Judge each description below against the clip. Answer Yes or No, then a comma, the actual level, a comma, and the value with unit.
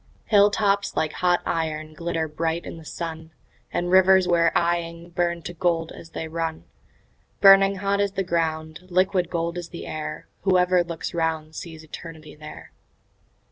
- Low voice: No, medium, 170 Hz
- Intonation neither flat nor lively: No, narrow, 2.1 semitones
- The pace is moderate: Yes, average, 165 wpm